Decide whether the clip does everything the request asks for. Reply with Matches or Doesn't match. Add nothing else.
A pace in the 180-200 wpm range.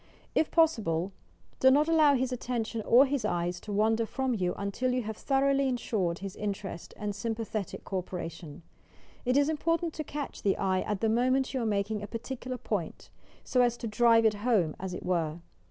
Matches